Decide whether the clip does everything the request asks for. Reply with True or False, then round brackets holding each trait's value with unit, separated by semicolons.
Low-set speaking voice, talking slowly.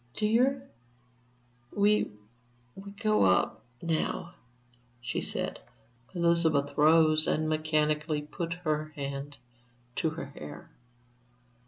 False (155 Hz; 100 wpm)